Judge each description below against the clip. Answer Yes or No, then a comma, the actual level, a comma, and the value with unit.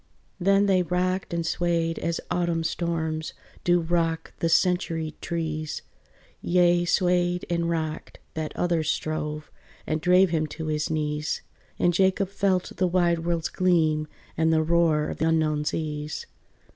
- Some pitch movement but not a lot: No, narrow, 2.0 semitones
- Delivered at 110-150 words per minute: Yes, average, 140 wpm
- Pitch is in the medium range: Yes, medium, 170 Hz